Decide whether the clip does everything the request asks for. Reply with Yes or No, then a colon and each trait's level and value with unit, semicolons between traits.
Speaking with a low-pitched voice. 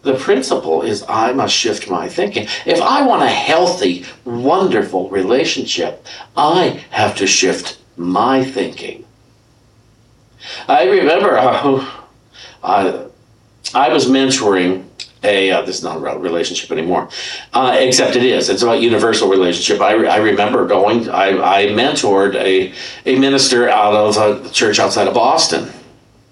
Yes: low, 120 Hz